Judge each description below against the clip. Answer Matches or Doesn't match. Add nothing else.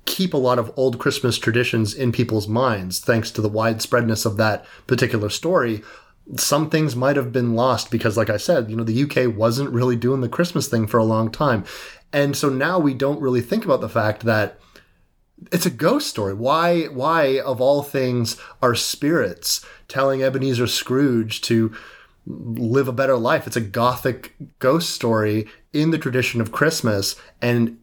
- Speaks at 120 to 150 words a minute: Doesn't match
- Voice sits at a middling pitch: Doesn't match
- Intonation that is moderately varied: Matches